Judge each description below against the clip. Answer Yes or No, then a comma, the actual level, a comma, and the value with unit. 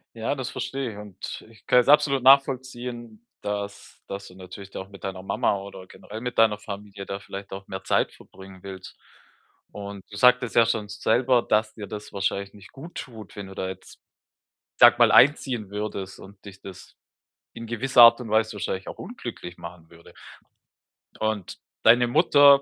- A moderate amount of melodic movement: Yes, average, 3.6 semitones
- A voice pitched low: Yes, low, 105 Hz